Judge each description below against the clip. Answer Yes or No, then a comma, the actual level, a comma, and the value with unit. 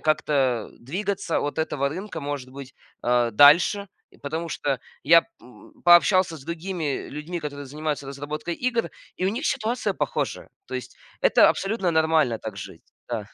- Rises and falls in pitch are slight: No, average, 4.2 semitones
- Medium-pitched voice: Yes, medium, 155 Hz